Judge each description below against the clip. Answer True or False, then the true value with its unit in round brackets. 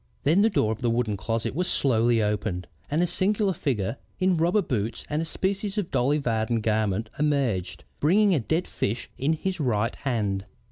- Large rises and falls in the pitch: True (7.7 semitones)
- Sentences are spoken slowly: False (185 wpm)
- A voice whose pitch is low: True (130 Hz)